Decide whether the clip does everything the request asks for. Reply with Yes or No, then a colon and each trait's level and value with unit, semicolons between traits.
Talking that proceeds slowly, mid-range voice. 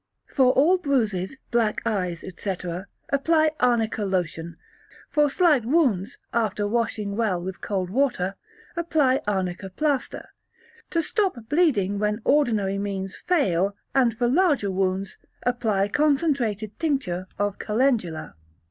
No: slow, 120 wpm; high, 220 Hz